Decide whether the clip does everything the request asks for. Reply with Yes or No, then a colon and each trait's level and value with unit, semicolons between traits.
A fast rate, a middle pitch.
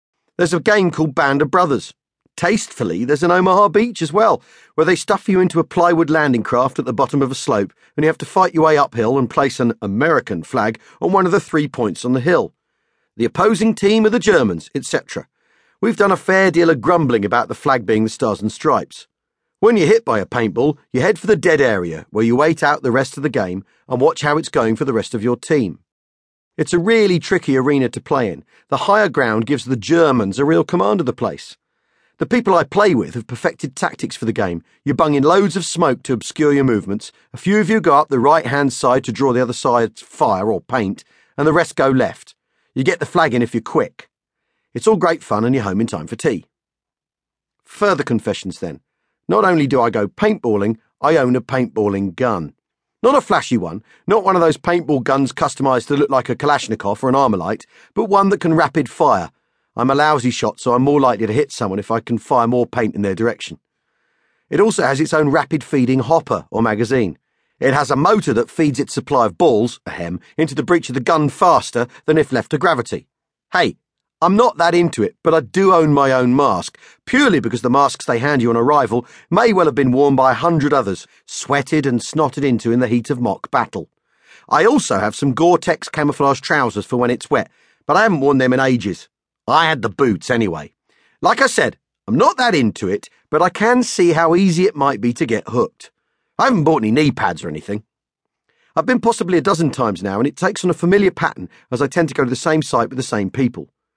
Yes: fast, 230 wpm; medium, 145 Hz